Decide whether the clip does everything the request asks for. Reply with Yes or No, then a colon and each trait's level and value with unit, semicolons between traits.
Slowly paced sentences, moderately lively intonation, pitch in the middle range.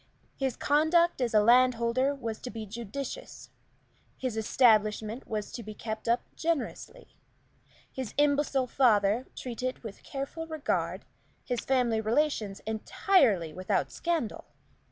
No: slow, 120 wpm; average, 4.2 semitones; high, 245 Hz